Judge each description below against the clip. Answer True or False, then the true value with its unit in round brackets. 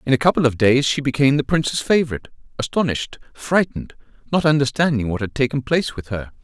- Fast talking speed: False (185 wpm)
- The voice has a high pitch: False (135 Hz)